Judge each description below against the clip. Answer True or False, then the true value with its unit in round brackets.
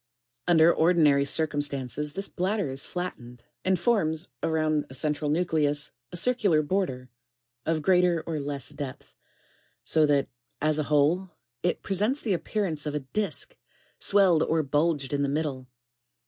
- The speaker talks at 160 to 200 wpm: False (150 wpm)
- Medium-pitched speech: True (155 Hz)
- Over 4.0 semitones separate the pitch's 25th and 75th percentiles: False (3.7 semitones)